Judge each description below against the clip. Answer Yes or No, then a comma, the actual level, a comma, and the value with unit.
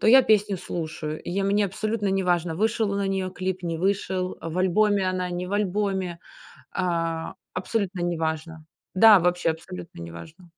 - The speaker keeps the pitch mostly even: No, average, 3.1 semitones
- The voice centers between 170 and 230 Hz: Yes, medium, 185 Hz